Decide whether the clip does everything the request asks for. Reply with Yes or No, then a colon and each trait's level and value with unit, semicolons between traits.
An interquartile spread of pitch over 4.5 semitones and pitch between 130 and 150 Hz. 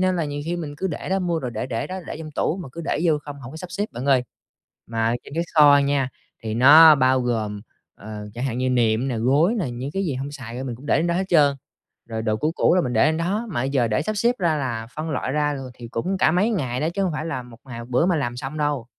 Yes: average, 5.2 semitones; medium, 140 Hz